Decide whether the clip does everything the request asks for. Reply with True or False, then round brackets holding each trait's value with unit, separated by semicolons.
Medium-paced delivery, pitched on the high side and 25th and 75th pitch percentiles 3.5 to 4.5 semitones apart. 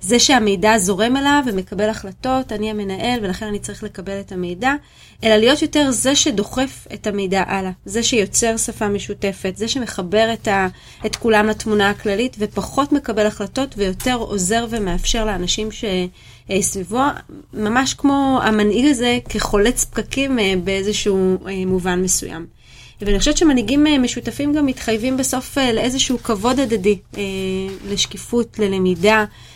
True (130 wpm; 215 Hz; 4.2 semitones)